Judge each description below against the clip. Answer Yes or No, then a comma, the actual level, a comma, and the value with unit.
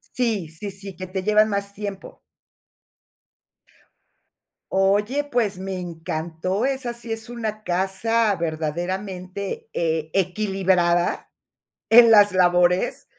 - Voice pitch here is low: No, high, 195 Hz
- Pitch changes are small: No, average, 3.3 semitones